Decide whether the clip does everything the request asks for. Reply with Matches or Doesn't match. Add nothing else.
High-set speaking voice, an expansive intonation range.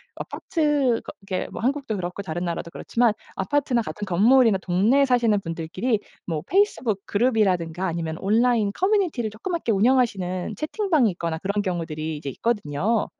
Matches